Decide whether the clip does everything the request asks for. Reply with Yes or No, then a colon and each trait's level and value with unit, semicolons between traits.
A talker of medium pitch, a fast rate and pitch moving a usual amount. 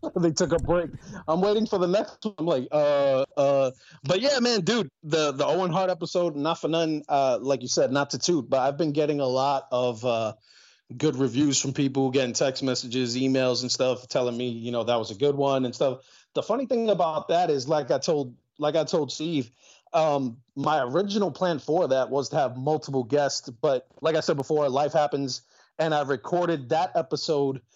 Yes: medium, 145 Hz; fast, 210 wpm; average, 3.9 semitones